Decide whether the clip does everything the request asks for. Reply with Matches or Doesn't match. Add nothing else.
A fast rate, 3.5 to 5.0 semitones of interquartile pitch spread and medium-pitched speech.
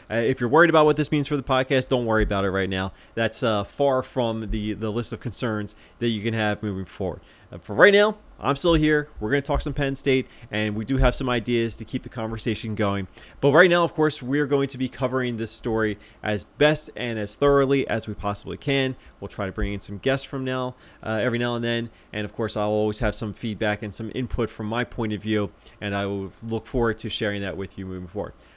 Doesn't match